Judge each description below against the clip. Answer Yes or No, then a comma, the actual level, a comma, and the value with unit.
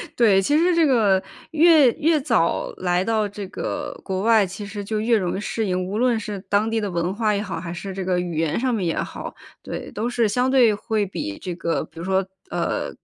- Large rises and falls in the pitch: No, average, 3.7 semitones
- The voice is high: Yes, high, 205 Hz